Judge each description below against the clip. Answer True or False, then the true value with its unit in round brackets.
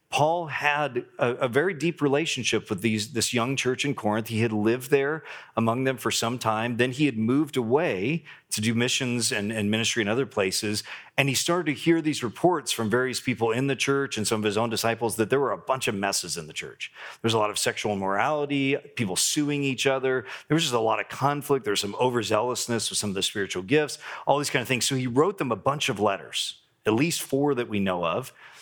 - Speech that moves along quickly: True (240 wpm)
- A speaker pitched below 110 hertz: False (125 Hz)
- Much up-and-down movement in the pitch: False (4.1 semitones)